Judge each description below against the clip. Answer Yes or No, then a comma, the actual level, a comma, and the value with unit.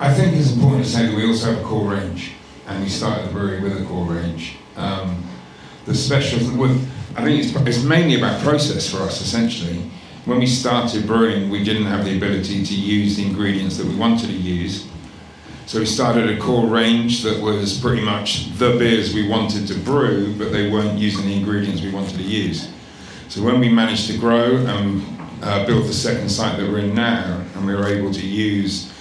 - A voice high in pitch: No, low, 105 Hz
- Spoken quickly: Yes, fast, 210 wpm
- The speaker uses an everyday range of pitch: Yes, average, 3.0 semitones